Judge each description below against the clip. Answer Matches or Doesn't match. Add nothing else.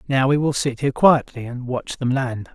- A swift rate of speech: Matches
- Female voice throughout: Doesn't match